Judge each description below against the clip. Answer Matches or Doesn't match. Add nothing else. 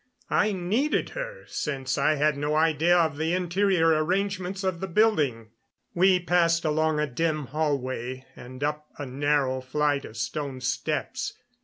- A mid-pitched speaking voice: Matches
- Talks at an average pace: Matches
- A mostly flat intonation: Doesn't match